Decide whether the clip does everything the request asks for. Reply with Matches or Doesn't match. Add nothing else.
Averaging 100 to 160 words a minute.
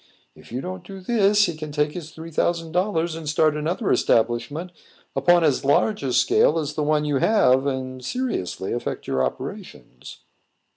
Doesn't match